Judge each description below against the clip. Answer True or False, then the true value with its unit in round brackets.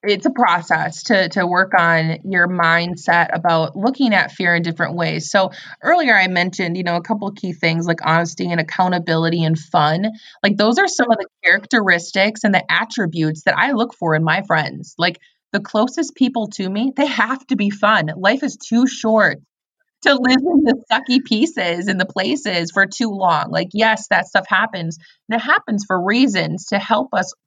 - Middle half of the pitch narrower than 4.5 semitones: False (4.9 semitones)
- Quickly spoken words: False (195 wpm)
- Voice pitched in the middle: False (195 Hz)